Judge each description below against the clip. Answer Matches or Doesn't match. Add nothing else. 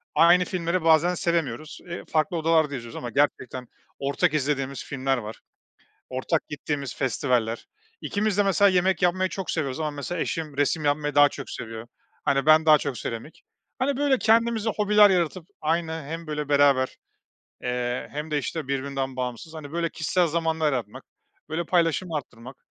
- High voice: Doesn't match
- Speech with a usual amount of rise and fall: Matches